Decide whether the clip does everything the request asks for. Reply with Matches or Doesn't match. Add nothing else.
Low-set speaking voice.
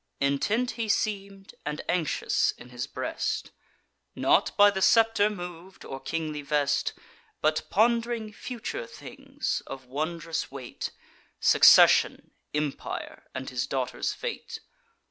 Doesn't match